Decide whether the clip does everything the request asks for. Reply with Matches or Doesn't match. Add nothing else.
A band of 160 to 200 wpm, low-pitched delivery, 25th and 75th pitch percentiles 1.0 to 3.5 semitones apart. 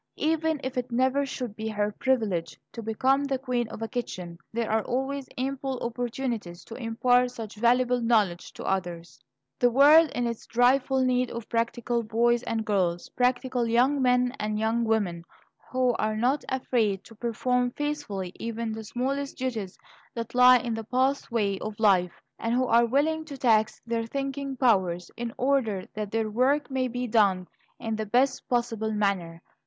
Doesn't match